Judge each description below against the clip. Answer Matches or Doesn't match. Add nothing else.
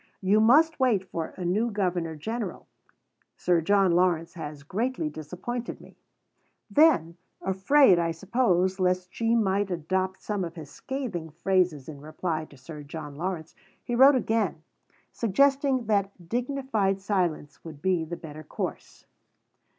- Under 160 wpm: Matches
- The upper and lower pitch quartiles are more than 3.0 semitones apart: Matches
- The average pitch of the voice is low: Doesn't match